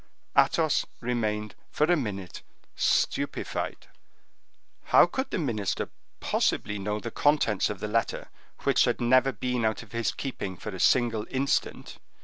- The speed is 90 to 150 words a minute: Yes, average, 140 wpm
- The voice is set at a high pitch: No, low, 115 Hz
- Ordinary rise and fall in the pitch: Yes, average, 3.5 semitones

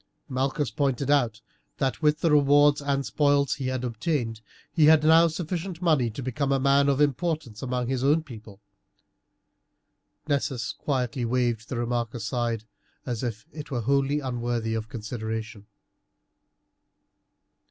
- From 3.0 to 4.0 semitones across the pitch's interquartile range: Yes, average, 3.6 semitones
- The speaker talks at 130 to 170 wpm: Yes, average, 140 wpm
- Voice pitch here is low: Yes, low, 130 Hz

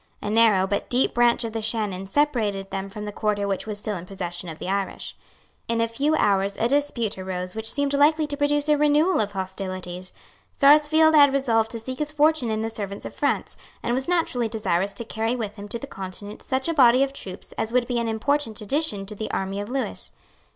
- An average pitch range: No, wide, 5.7 semitones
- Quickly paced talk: Yes, fast, 225 wpm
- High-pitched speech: Yes, high, 225 Hz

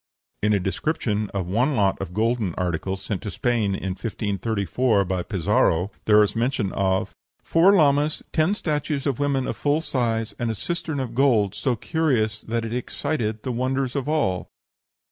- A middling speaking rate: Yes, average, 170 wpm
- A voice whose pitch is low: Yes, low, 115 Hz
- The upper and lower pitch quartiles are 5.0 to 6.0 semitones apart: Yes, wide, 5.6 semitones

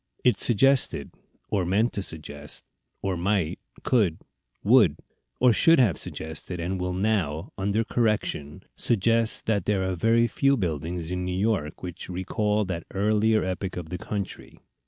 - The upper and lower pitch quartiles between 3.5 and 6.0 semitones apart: Yes, average, 3.9 semitones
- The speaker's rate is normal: Yes, average, 150 wpm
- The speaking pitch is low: Yes, very low, 95 Hz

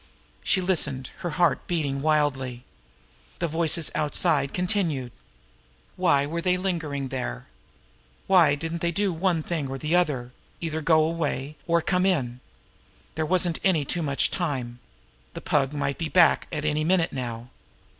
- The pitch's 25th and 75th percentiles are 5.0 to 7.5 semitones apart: No, average, 3.9 semitones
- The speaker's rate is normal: Yes, average, 150 wpm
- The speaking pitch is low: No, medium, 155 Hz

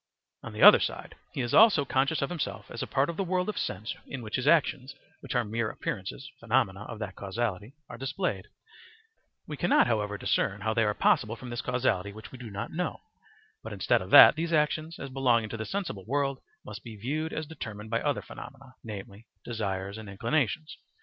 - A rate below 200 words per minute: No, fast, 205 wpm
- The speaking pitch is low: Yes, low, 120 Hz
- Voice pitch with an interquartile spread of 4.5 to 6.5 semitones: Yes, average, 5.2 semitones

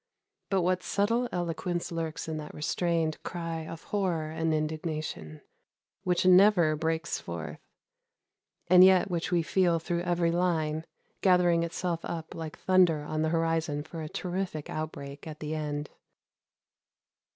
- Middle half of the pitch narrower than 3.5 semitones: Yes, narrow, 2.4 semitones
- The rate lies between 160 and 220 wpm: No, average, 140 wpm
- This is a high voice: No, medium, 165 Hz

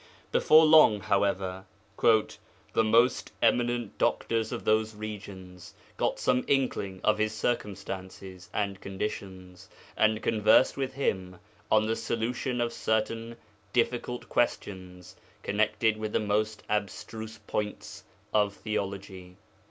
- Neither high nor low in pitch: No, low, 105 Hz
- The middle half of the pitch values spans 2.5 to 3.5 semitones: Yes, average, 2.8 semitones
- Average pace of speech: No, slow, 115 wpm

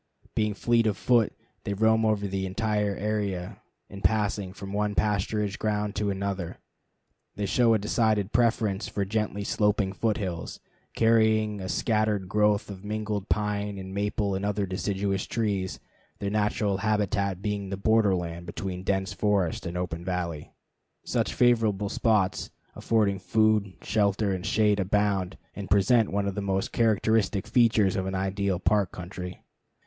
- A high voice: No, low, 100 Hz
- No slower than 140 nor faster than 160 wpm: Yes, average, 155 wpm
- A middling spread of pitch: No, narrow, 2.0 semitones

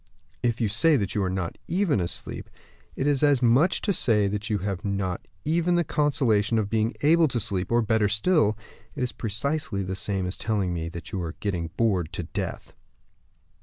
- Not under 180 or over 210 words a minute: Yes, fast, 205 wpm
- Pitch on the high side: No, low, 110 Hz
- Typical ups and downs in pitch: No, wide, 6.2 semitones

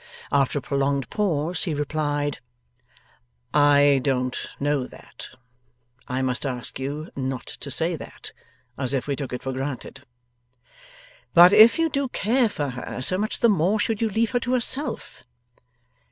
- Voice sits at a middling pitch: Yes, medium, 145 Hz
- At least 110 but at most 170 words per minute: Yes, average, 155 wpm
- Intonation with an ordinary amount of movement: No, wide, 7.5 semitones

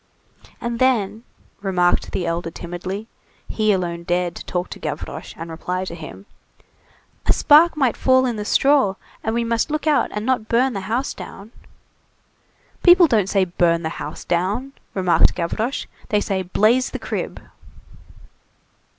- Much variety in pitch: Yes, wide, 5.7 semitones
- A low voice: No, high, 210 Hz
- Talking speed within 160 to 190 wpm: No, average, 150 wpm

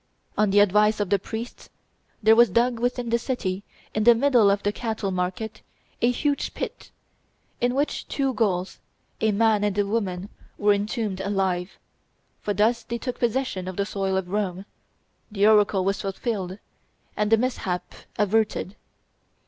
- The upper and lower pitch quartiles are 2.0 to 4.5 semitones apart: Yes, average, 3.0 semitones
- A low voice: No, high, 210 Hz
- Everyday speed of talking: Yes, average, 160 wpm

